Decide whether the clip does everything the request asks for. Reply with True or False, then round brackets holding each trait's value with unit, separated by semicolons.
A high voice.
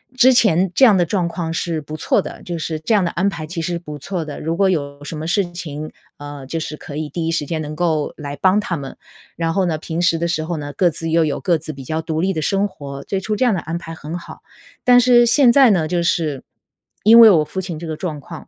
False (165 Hz)